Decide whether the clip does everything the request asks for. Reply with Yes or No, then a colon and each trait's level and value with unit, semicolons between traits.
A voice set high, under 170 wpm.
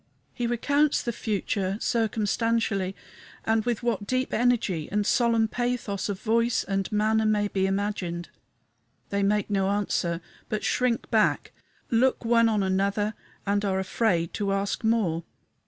Yes: high, 210 Hz; average, 140 wpm